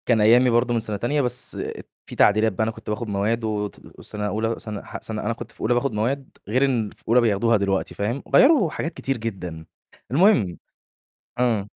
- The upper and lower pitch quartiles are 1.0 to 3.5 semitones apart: Yes, average, 2.9 semitones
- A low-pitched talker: Yes, low, 115 Hz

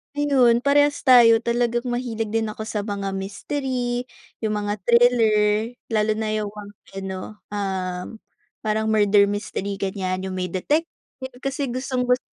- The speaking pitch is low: No, high, 220 Hz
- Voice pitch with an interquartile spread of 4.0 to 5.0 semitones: No, average, 3.3 semitones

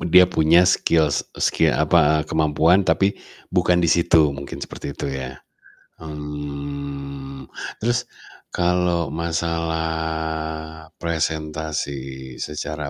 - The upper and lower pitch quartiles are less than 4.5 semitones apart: Yes, narrow, 2.5 semitones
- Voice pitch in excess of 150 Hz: No, very low, 80 Hz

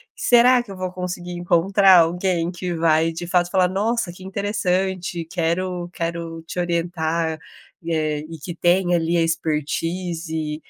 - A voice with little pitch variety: Yes, narrow, 2.0 semitones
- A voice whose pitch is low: No, medium, 175 Hz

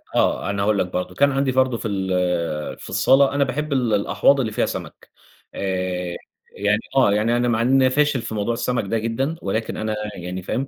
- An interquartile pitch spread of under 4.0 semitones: No, average, 4.7 semitones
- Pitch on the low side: Yes, low, 115 Hz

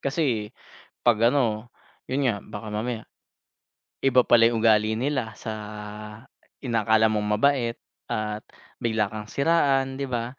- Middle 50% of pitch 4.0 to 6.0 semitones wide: No, average, 3.6 semitones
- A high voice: No, low, 115 Hz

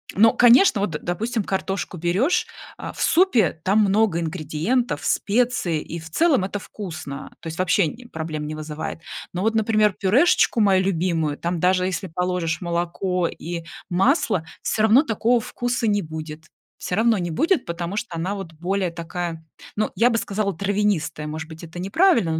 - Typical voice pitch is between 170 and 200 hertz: Yes, medium, 185 Hz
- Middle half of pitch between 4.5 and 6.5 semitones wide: Yes, average, 4.8 semitones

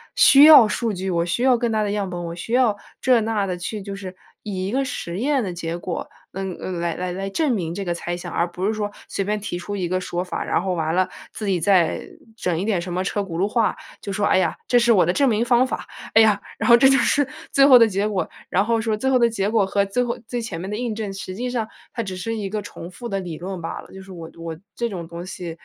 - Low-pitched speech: No, high, 200 Hz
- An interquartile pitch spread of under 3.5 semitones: No, average, 4.2 semitones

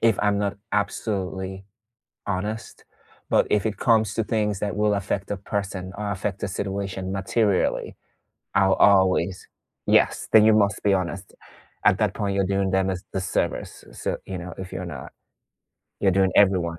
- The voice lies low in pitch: Yes, low, 100 Hz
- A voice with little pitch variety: Yes, narrow, 1.6 semitones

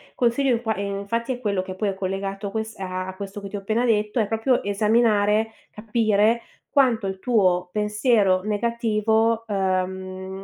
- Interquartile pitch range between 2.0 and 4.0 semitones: Yes, average, 2.7 semitones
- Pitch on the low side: No, high, 210 Hz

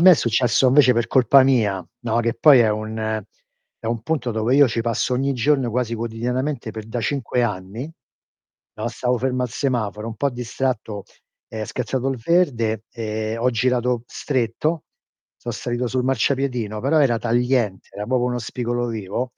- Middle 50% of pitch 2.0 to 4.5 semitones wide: Yes, narrow, 2.6 semitones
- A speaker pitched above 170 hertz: No, low, 120 Hz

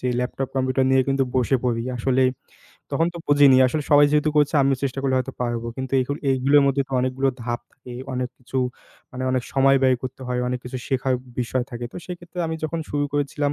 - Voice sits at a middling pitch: No, low, 130 Hz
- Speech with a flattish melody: Yes, narrow, 1.9 semitones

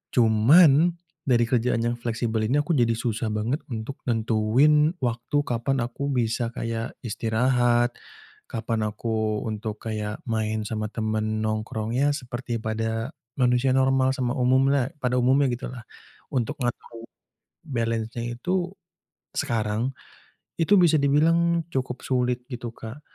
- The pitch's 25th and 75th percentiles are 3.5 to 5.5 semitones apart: No, average, 3.0 semitones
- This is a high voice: No, low, 120 Hz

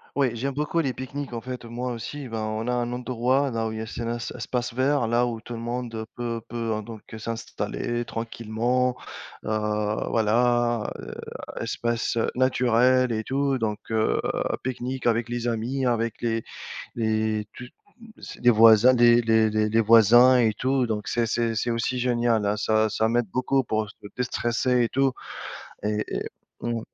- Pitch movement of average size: No, narrow, 2.0 semitones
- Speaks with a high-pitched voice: No, low, 120 Hz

